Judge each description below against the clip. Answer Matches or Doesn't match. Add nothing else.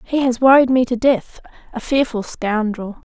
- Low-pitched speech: Doesn't match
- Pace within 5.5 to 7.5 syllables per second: Doesn't match